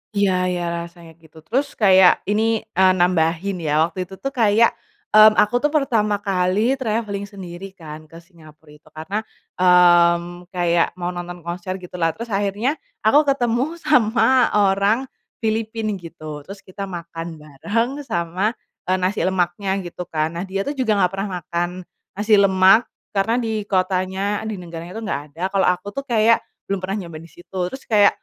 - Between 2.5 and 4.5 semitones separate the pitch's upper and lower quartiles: Yes, average, 3.6 semitones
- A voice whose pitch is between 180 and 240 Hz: Yes, high, 190 Hz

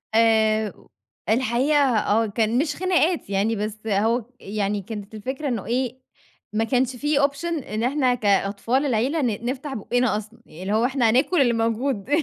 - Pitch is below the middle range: No, high, 230 Hz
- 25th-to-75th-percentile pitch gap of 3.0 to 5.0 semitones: Yes, average, 3.7 semitones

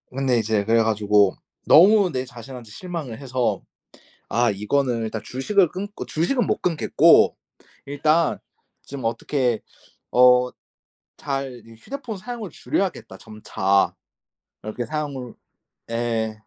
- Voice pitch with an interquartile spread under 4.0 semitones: No, wide, 5.6 semitones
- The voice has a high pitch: No, low, 125 Hz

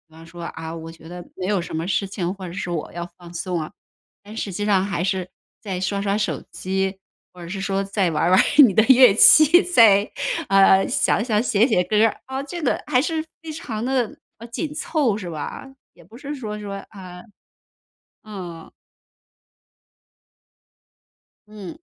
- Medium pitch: No, high, 195 Hz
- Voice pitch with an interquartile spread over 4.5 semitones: No, average, 4.1 semitones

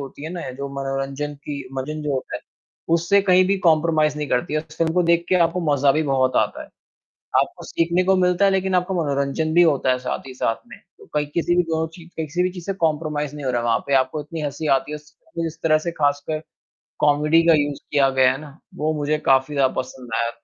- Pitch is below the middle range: No, medium, 150 Hz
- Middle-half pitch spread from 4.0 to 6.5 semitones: No, average, 3.3 semitones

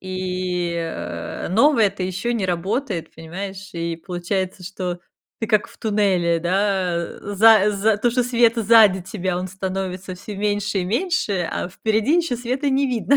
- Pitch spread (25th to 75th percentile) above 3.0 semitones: Yes, average, 3.5 semitones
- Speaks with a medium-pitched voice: No, high, 195 Hz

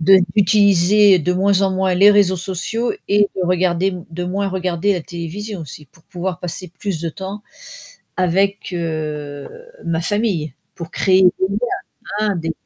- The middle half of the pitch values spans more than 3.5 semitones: No, average, 2.9 semitones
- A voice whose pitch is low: No, medium, 185 Hz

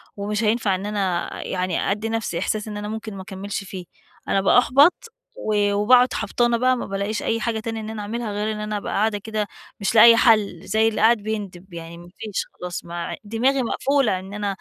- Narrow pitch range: Yes, narrow, 2.3 semitones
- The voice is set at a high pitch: Yes, high, 210 Hz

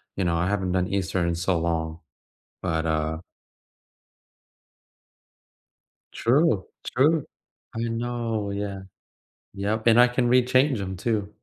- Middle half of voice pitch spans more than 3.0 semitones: Yes, average, 4.9 semitones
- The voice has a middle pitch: No, low, 100 Hz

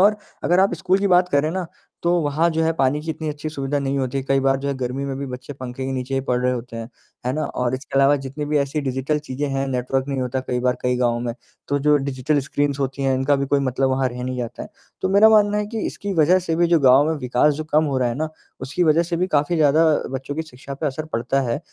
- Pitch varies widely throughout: No, average, 3.2 semitones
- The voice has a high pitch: No, medium, 140 Hz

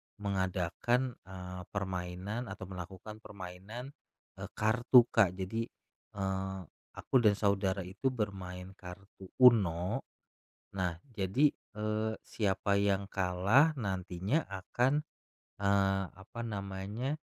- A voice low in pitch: Yes, low, 100 Hz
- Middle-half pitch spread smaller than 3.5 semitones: Yes, average, 2.7 semitones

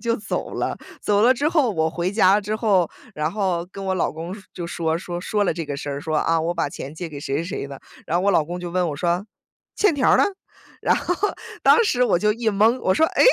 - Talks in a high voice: No, medium, 180 Hz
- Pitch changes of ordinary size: Yes, average, 4.4 semitones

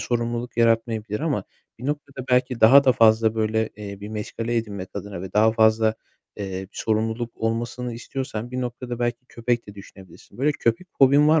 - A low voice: Yes, low, 115 Hz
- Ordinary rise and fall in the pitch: No, narrow, 2.3 semitones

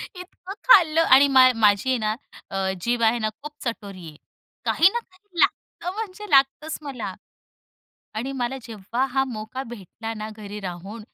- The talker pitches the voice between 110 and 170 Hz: No, high, 245 Hz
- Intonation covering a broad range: Yes, wide, 6.3 semitones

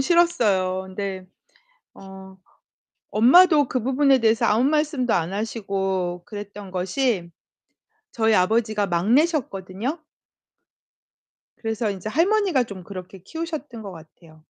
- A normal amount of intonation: No, wide, 5.8 semitones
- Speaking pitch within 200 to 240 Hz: Yes, high, 215 Hz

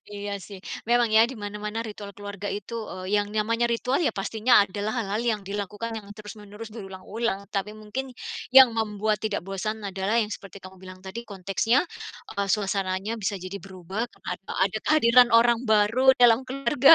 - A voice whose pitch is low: No, high, 210 Hz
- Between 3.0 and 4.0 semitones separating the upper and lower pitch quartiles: No, narrow, 2.6 semitones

